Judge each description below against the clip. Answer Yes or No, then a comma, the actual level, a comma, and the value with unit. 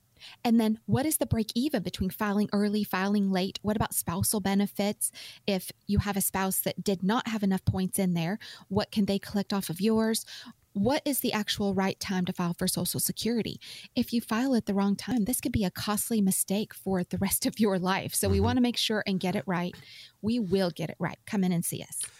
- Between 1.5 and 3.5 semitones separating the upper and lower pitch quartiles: Yes, average, 2.9 semitones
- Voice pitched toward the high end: Yes, high, 200 Hz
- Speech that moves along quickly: Yes, fast, 230 wpm